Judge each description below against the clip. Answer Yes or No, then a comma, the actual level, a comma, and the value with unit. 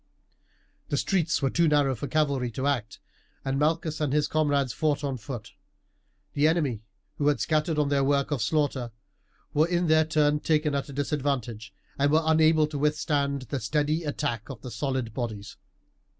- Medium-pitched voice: Yes, medium, 145 Hz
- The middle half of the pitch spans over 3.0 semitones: No, narrow, 2.6 semitones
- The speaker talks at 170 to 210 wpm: Yes, average, 175 wpm